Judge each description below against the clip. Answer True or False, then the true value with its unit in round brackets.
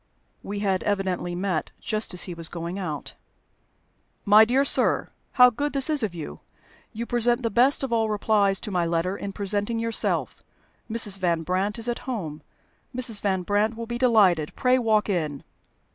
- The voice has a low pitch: False (205 Hz)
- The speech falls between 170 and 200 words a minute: True (175 wpm)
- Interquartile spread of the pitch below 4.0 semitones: False (4.3 semitones)